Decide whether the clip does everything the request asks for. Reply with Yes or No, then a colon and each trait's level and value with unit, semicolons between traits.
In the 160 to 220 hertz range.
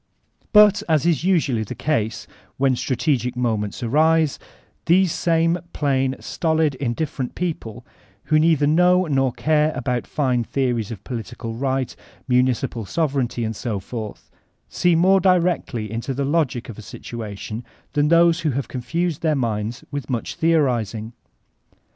No: low, 135 Hz